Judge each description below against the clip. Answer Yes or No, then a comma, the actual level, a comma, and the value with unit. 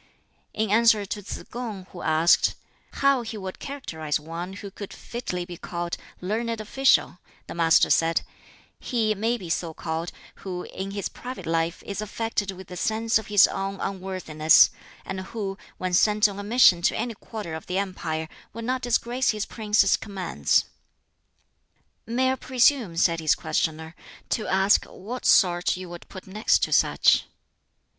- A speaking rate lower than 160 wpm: No, average, 165 wpm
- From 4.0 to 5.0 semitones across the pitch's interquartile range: Yes, average, 4.3 semitones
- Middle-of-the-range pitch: No, high, 195 Hz